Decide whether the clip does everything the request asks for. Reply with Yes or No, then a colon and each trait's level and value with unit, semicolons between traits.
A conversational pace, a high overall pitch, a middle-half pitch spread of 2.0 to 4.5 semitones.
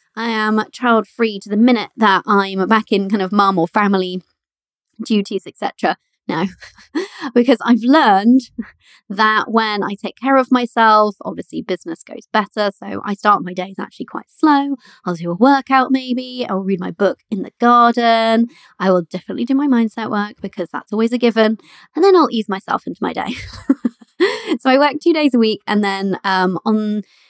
Yes: average, 185 wpm; high, 220 Hz; average, 3.7 semitones